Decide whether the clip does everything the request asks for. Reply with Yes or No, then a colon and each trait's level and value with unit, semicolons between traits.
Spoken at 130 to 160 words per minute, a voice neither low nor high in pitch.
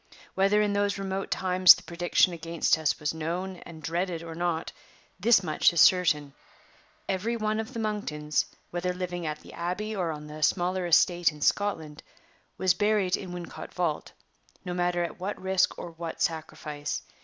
No: average, 170 wpm; medium, 175 Hz